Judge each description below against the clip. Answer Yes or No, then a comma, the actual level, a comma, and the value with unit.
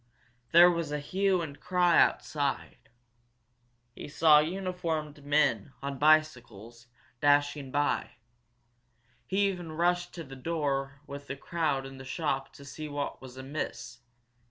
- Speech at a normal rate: No, slow, 130 wpm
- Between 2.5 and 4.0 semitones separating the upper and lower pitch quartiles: Yes, average, 3.6 semitones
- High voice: No, medium, 145 Hz